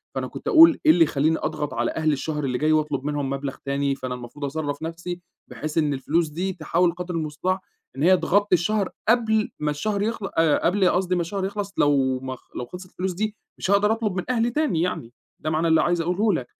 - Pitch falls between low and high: Yes, medium, 165 Hz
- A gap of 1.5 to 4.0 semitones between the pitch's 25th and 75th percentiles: No, average, 4.7 semitones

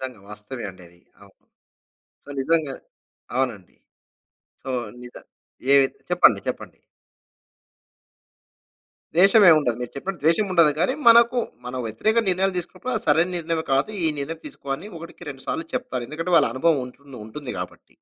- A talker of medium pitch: Yes, medium, 155 Hz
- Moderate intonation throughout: No, wide, 5.9 semitones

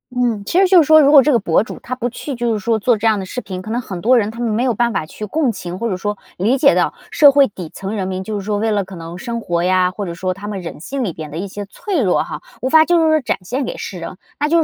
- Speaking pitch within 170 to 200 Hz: No, high, 215 Hz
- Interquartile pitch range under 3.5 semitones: No, average, 5.2 semitones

